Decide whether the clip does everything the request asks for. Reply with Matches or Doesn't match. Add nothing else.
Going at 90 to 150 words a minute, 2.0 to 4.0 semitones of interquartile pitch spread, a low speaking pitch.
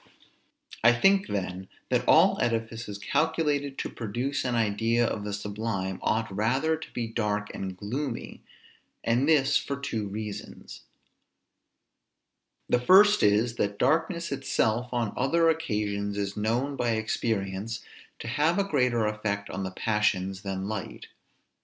Doesn't match